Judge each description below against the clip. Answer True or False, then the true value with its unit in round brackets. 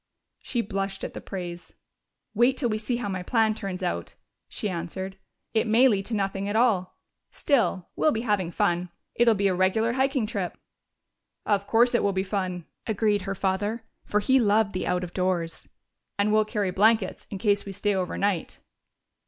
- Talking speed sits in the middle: True (185 wpm)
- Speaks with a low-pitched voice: False (200 Hz)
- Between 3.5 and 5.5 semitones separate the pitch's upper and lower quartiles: False (2.9 semitones)